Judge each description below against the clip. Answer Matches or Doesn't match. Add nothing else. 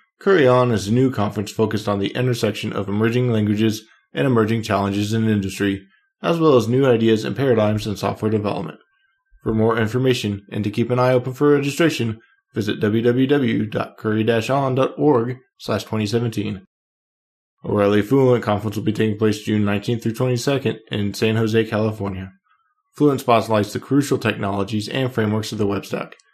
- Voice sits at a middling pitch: Doesn't match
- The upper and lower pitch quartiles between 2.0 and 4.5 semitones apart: Matches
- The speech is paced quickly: Doesn't match